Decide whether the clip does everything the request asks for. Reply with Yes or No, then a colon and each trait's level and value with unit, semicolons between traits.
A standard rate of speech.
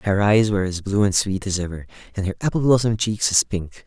No: fast, 250 wpm